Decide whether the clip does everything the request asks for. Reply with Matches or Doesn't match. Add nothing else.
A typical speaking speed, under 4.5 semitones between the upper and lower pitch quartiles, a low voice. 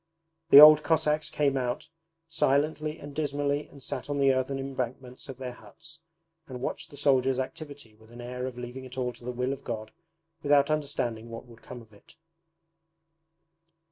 Matches